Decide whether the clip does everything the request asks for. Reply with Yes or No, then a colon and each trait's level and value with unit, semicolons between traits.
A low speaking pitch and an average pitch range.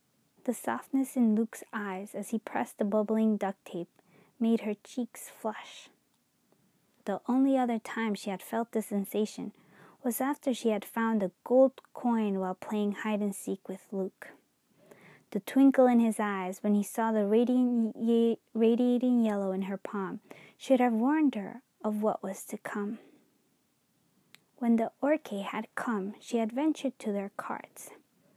No: high, 225 Hz; average, 3.1 semitones